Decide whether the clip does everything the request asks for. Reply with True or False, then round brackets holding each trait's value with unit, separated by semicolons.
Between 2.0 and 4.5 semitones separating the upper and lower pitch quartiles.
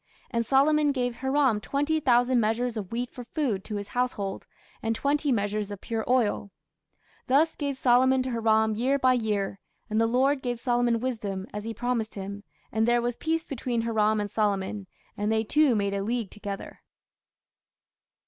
True (3.5 semitones)